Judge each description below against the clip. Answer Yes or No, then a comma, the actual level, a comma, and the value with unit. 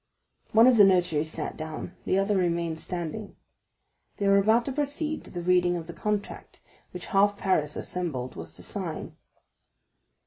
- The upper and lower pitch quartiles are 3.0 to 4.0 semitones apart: Yes, average, 3.7 semitones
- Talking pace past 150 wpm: Yes, average, 165 wpm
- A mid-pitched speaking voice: Yes, medium, 180 Hz